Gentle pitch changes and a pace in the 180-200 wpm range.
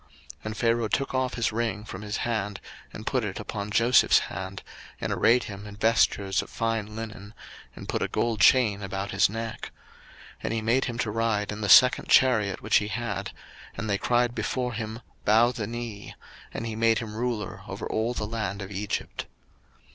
Yes: narrow, 2.2 semitones; average, 195 wpm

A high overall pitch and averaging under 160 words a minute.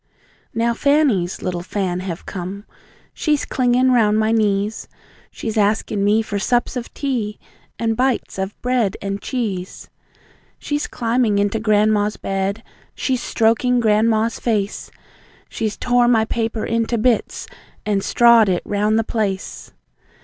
Yes: high, 220 Hz; slow, 135 wpm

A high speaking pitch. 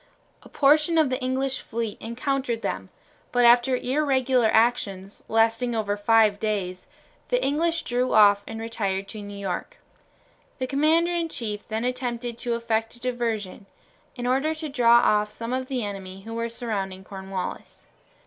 Yes: high, 235 Hz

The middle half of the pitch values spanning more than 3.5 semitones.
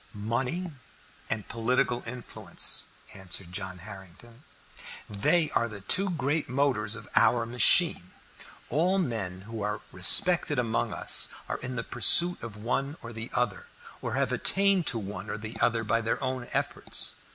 Yes: average, 4.6 semitones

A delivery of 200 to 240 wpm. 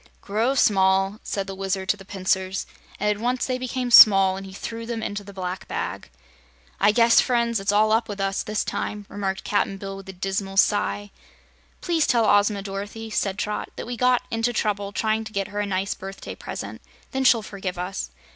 Yes: fast, 205 wpm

